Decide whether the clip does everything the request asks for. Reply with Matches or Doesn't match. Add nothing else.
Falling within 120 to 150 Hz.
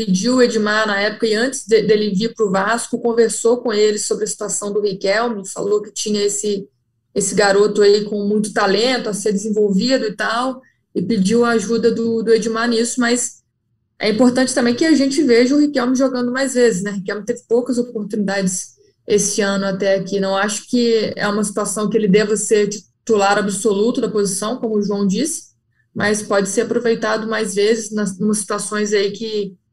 Doesn't match